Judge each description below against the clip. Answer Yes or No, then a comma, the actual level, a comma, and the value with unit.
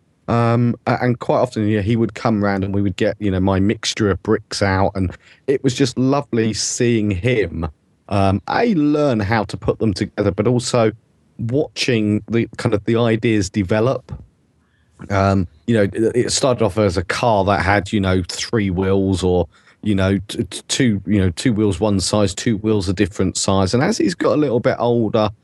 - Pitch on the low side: Yes, low, 105 Hz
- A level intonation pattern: No, average, 3.1 semitones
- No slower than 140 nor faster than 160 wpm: No, average, 200 wpm